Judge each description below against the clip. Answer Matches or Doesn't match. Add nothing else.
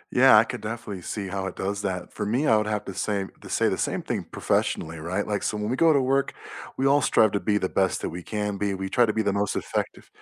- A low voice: Matches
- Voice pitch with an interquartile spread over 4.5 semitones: Doesn't match